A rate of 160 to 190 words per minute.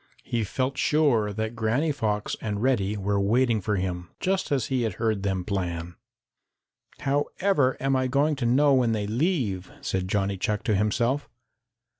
Yes: average, 165 wpm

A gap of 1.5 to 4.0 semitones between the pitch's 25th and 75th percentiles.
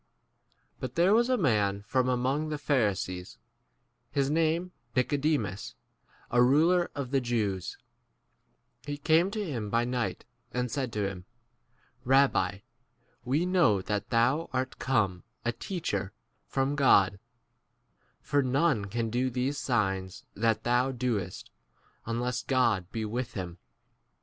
No: average, 5.2 semitones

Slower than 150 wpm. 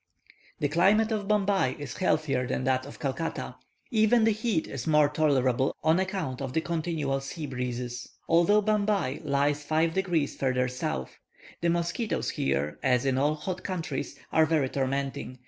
No: average, 160 wpm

